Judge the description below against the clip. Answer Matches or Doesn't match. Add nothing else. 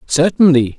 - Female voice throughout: Doesn't match